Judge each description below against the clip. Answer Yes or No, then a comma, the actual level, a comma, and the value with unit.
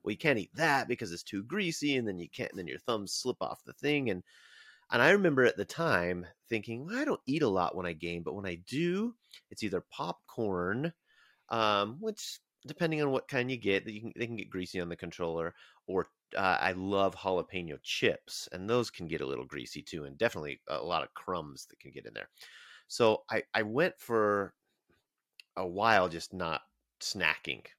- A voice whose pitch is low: Yes, low, 100 Hz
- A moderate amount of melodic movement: No, wide, 6.1 semitones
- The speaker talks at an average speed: No, fast, 210 wpm